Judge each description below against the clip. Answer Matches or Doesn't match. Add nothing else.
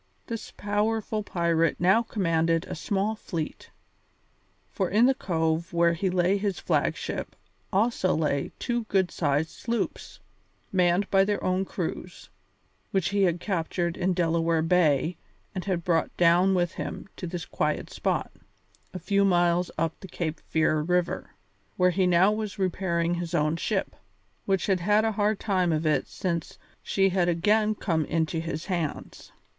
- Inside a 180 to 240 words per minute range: Doesn't match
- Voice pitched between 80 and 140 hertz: Doesn't match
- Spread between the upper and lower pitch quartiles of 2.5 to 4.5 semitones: Matches